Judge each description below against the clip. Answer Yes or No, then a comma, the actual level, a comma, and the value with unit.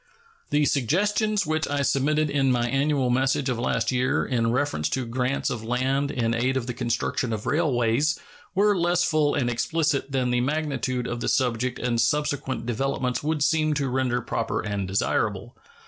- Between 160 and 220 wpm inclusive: Yes, average, 175 wpm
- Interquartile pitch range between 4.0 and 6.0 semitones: No, average, 3.5 semitones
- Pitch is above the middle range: No, low, 130 Hz